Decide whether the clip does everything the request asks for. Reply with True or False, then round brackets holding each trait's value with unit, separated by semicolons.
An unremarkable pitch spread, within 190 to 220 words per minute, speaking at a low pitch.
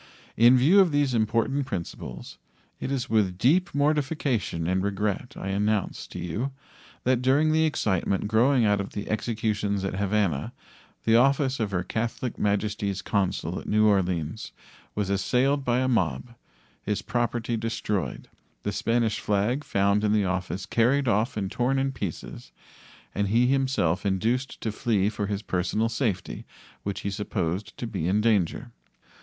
False (4.1 semitones; 155 wpm; 110 Hz)